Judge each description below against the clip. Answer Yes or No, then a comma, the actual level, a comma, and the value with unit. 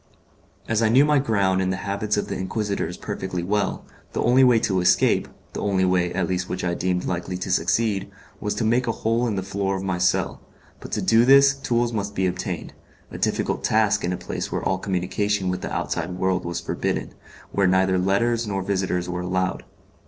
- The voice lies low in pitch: Yes, very low, 95 Hz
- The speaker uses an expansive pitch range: No, average, 3.0 semitones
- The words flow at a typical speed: No, fast, 210 wpm